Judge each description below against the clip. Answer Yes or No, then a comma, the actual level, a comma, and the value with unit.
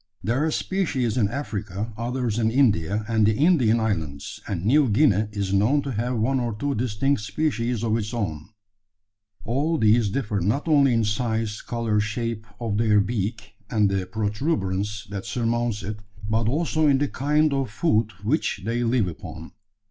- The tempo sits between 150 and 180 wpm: Yes, average, 170 wpm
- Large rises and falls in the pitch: No, average, 3.7 semitones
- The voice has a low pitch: Yes, low, 115 Hz